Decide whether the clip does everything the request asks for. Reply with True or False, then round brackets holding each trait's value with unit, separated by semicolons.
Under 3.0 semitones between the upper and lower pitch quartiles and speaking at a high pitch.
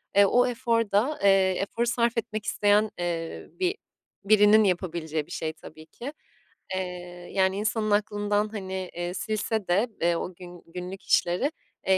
False (3.4 semitones; 195 Hz)